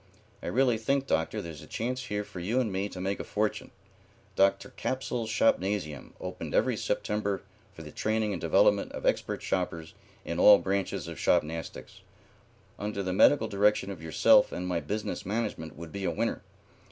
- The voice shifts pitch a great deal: No, average, 3.5 semitones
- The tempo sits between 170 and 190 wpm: Yes, average, 175 wpm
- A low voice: Yes, low, 100 Hz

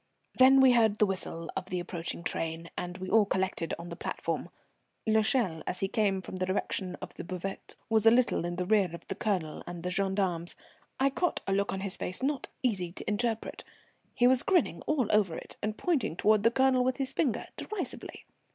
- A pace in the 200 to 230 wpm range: Yes, fast, 205 wpm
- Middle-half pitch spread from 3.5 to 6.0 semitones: Yes, average, 4.9 semitones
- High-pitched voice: Yes, high, 200 Hz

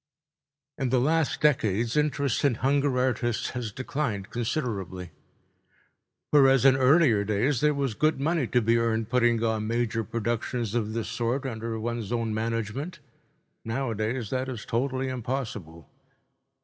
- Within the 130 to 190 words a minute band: Yes, slow, 135 wpm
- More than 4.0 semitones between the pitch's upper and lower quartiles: No, average, 3.2 semitones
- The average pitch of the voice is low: Yes, low, 120 Hz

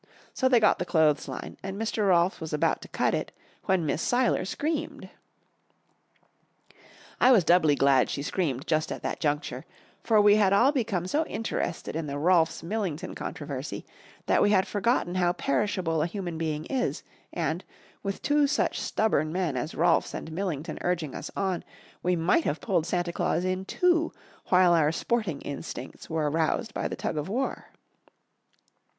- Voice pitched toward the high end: No, medium, 180 Hz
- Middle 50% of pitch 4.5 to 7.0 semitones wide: Yes, average, 4.9 semitones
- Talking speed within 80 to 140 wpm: No, average, 170 wpm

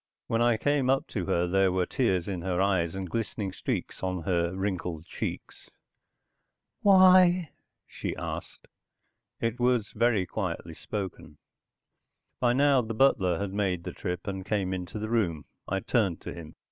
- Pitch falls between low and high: No, low, 100 Hz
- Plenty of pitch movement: No, average, 4.6 semitones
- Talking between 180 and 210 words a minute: No, average, 160 wpm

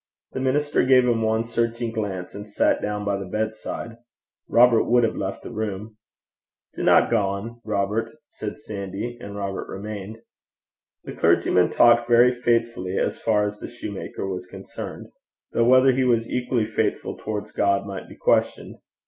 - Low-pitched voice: Yes, low, 110 Hz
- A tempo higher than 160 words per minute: No, average, 155 wpm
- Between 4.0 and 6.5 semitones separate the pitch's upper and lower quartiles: No, average, 2.8 semitones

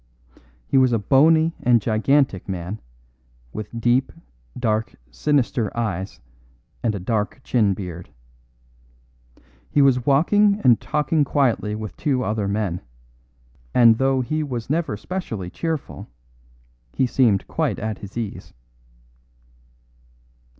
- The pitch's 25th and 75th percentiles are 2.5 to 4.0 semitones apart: No, average, 4.8 semitones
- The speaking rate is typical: No, slow, 115 wpm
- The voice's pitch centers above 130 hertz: No, low, 120 Hz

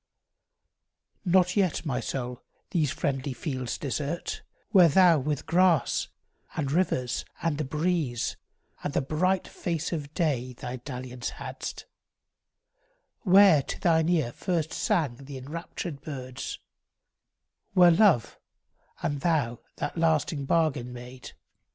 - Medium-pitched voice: Yes, medium, 150 Hz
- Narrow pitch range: No, average, 4.8 semitones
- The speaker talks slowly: Yes, slow, 120 wpm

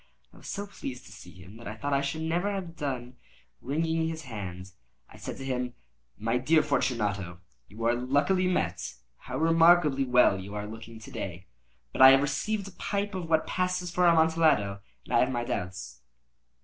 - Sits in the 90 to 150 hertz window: Yes, low, 135 Hz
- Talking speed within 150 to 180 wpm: No, average, 190 wpm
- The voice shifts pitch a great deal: Yes, wide, 6.8 semitones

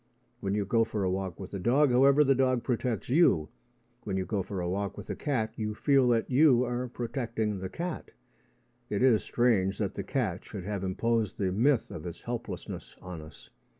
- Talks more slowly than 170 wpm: No, fast, 205 wpm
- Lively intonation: No, average, 4.7 semitones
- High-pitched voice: No, low, 110 Hz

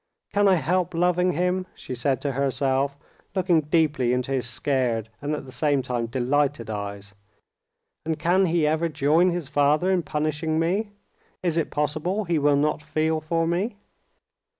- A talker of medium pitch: Yes, medium, 150 Hz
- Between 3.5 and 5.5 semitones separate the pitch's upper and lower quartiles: Yes, average, 4.0 semitones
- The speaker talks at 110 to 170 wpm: Yes, average, 165 wpm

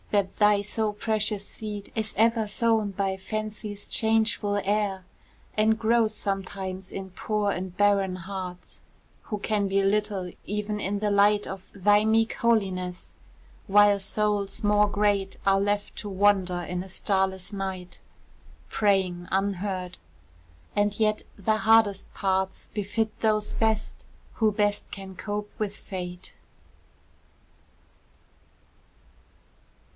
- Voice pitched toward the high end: Yes, high, 205 Hz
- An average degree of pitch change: No, narrow, 1.8 semitones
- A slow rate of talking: Yes, slow, 120 wpm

